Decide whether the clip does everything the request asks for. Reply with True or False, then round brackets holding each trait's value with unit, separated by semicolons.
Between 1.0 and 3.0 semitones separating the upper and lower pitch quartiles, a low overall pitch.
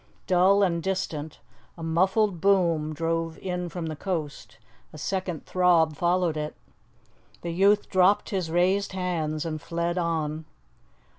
False (2.7 semitones; 170 Hz)